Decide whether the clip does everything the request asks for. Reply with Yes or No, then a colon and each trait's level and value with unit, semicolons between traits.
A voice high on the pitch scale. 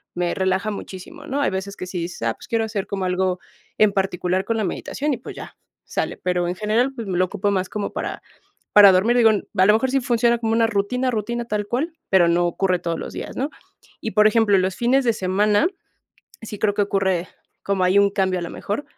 Yes: high, 200 Hz